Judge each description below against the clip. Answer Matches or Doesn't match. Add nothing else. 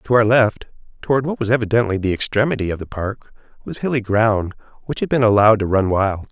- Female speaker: Doesn't match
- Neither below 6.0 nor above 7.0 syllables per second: Matches